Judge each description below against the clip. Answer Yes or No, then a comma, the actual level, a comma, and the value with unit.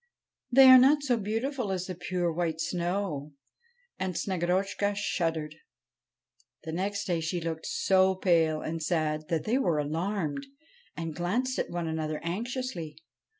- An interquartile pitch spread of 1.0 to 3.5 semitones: No, average, 4.1 semitones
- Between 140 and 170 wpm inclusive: Yes, average, 150 wpm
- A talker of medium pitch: Yes, medium, 180 Hz